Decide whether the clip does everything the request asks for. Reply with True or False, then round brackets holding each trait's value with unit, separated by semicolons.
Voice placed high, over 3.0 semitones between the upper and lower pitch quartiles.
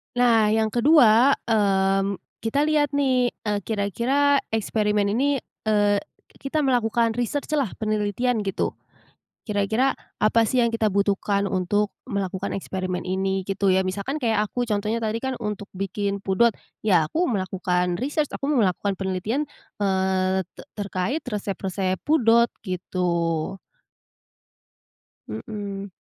True (210 Hz; 3.7 semitones)